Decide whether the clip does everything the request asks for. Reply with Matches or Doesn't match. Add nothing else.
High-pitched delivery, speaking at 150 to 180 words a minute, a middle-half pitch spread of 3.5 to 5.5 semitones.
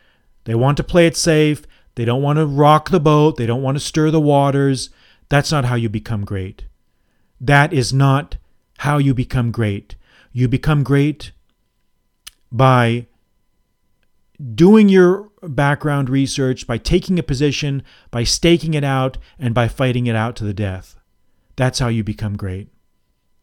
Doesn't match